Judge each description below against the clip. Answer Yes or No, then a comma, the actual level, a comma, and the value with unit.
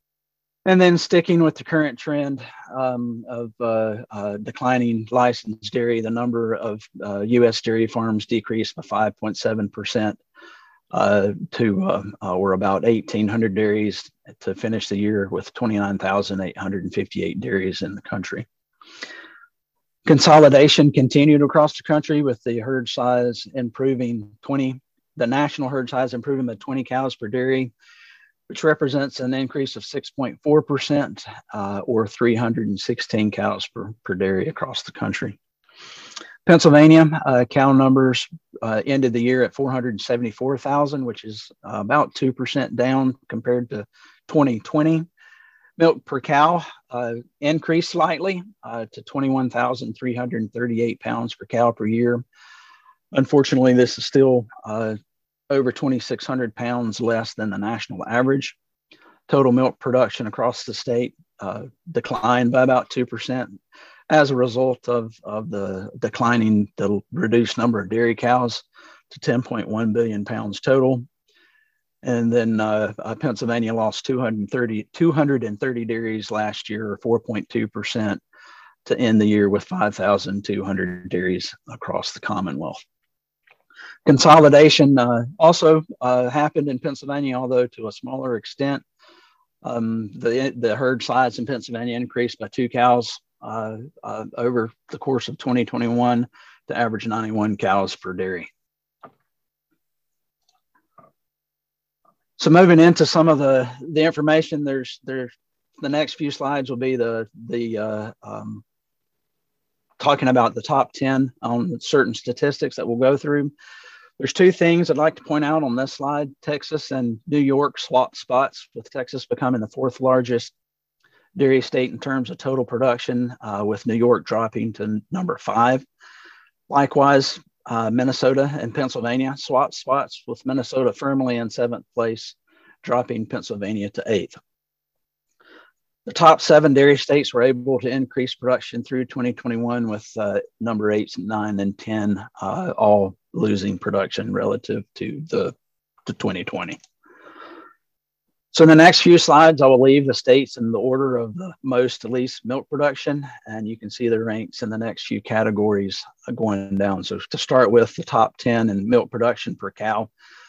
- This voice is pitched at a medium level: No, low, 125 Hz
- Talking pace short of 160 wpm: Yes, average, 140 wpm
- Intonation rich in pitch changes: No, average, 4.0 semitones